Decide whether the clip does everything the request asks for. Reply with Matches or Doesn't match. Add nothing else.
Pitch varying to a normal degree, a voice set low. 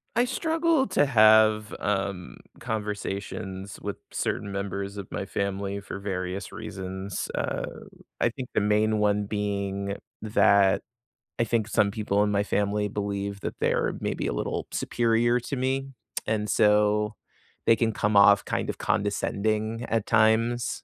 Doesn't match